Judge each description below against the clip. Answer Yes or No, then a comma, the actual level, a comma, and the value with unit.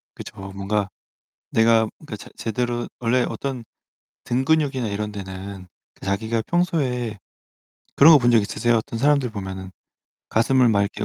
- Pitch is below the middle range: Yes, low, 115 Hz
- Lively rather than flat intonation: No, average, 3.8 semitones